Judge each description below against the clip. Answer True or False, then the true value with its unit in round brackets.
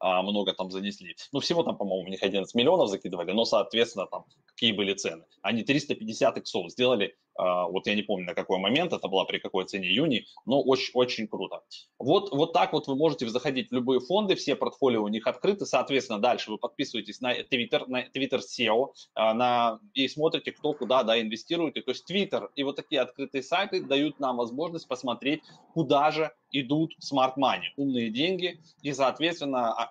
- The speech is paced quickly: True (180 wpm)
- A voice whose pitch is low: True (125 Hz)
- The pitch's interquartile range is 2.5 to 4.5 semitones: False (4.9 semitones)